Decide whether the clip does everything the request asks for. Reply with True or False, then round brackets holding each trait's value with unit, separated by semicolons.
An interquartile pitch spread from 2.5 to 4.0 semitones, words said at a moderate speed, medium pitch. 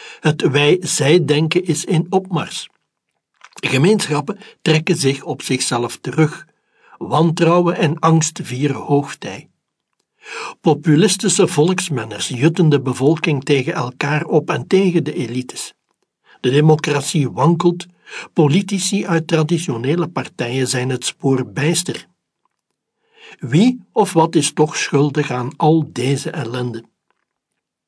False (3.6 semitones; 105 wpm; 155 Hz)